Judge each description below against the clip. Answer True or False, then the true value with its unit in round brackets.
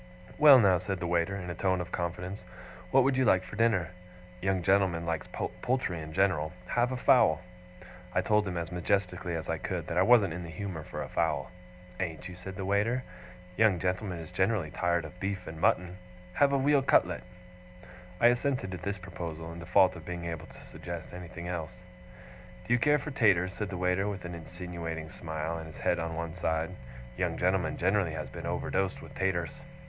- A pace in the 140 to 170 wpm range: False (200 wpm)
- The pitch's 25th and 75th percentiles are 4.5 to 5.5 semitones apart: False (3.0 semitones)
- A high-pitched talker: False (90 Hz)